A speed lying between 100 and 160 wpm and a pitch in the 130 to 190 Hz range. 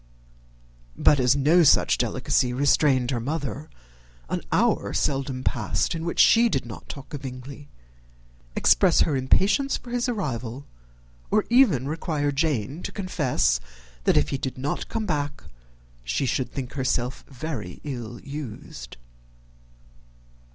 Yes: slow, 135 wpm; medium, 140 Hz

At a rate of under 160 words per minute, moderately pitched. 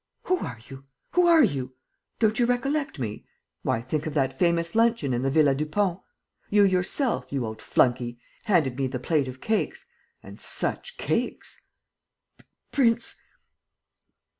Yes: average, 145 wpm; medium, 160 Hz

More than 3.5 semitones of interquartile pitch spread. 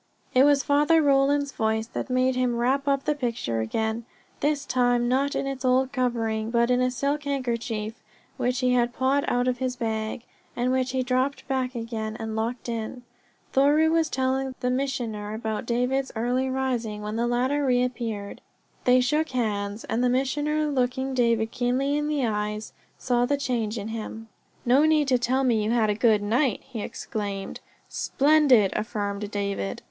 No: average, 3.2 semitones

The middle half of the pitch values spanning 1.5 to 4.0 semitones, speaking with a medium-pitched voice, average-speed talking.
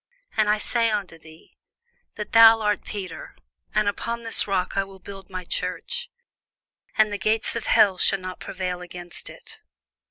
No: average, 3.0 semitones; high, 205 Hz; average, 170 wpm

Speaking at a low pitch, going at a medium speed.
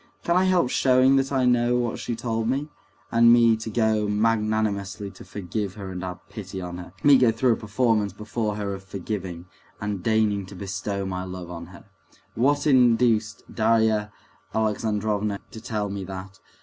Yes: low, 105 Hz; average, 175 wpm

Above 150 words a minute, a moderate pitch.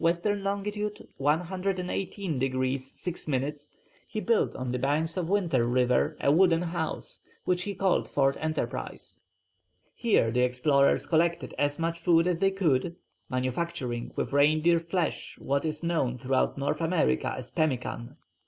No: average, 140 wpm; medium, 155 Hz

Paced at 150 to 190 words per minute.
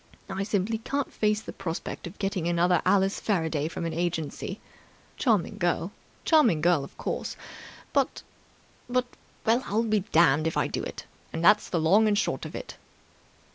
Yes: average, 170 wpm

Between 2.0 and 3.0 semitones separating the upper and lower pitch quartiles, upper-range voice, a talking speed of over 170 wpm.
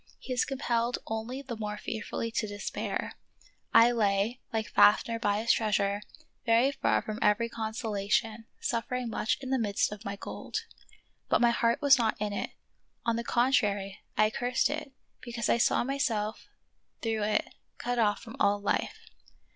No: narrow, 2.4 semitones; high, 225 Hz; average, 165 wpm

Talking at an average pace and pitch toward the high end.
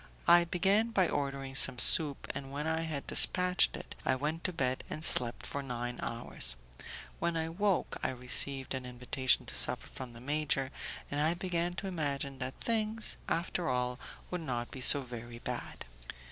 No: average, 175 wpm; medium, 140 Hz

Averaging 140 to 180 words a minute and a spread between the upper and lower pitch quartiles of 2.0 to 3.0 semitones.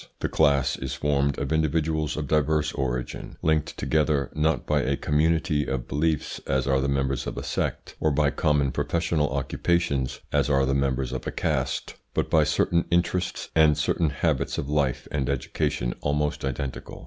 Yes: average, 170 wpm; narrow, 2.4 semitones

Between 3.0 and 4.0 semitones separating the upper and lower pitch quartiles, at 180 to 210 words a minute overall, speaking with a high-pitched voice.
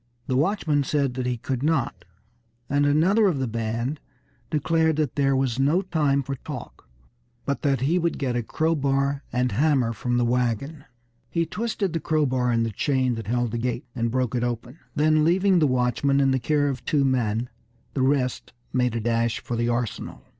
No: average, 3.7 semitones; average, 190 wpm; low, 135 Hz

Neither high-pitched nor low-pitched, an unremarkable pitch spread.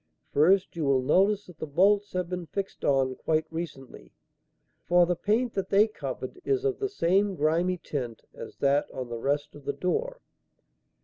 No: medium, 175 Hz; wide, 5.8 semitones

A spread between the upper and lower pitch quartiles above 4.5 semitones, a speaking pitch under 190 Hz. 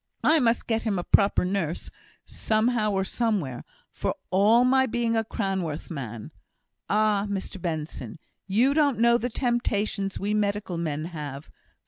No: average, 4.9 semitones; high, 205 Hz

